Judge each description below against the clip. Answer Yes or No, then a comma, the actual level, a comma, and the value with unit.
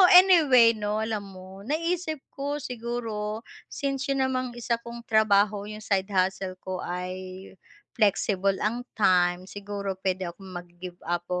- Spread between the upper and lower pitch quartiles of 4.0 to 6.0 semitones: Yes, average, 4.3 semitones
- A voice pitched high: Yes, high, 210 Hz